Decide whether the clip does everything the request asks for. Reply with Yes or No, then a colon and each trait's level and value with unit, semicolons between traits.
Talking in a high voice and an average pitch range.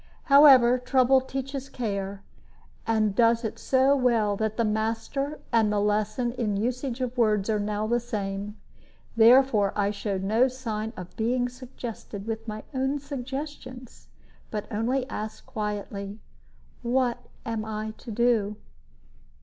Yes: high, 230 Hz; average, 3.2 semitones